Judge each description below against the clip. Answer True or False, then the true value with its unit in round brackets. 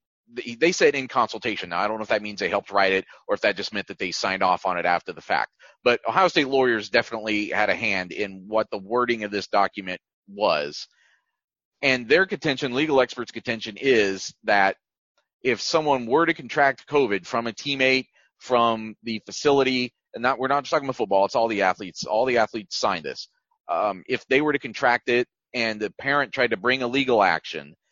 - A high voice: False (115 Hz)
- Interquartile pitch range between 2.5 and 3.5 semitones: False (4.3 semitones)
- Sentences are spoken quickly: True (210 wpm)